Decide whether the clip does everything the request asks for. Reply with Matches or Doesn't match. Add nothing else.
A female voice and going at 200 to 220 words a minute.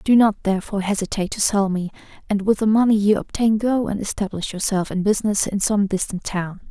Matches